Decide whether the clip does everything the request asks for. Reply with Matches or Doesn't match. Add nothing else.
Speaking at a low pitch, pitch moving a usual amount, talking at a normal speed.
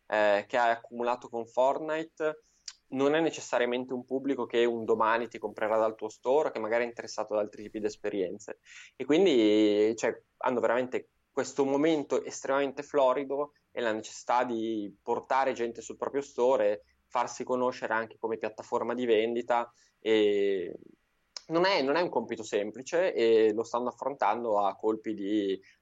Matches